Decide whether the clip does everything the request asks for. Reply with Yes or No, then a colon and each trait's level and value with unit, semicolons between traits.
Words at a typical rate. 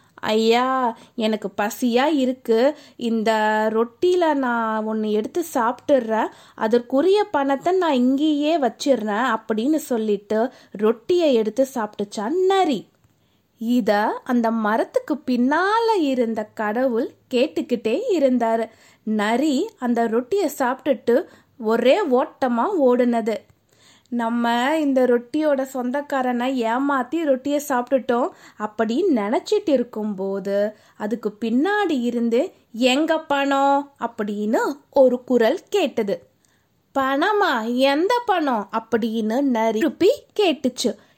Yes: average, 90 wpm